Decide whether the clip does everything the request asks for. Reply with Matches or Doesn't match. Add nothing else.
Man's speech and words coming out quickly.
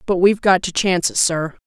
Doesn't match